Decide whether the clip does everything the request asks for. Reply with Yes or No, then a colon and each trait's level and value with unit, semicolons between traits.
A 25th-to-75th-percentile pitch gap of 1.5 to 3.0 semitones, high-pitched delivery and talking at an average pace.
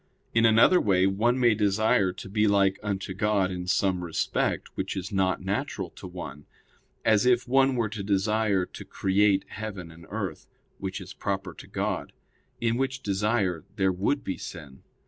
No: average, 2.7 semitones; low, 100 Hz; average, 170 wpm